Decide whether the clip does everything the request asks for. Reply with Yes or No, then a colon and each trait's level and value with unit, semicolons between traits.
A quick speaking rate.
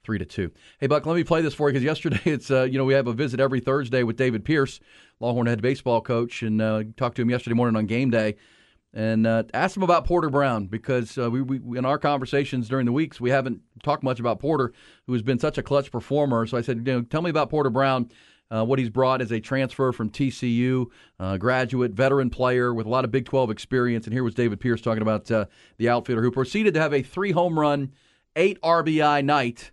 Yes: fast, 245 wpm